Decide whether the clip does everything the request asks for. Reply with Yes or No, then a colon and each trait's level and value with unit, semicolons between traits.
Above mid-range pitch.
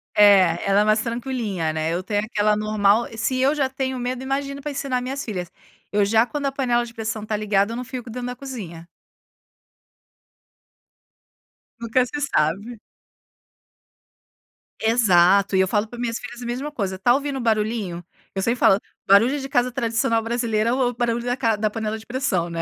Yes: high, 230 Hz